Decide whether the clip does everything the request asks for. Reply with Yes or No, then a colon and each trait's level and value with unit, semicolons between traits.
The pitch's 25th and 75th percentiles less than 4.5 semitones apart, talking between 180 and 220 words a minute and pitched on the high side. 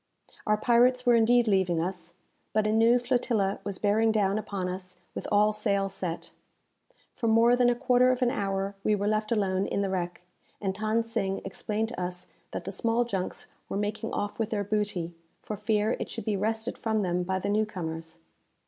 Yes: average, 2.8 semitones; average, 200 wpm; high, 210 Hz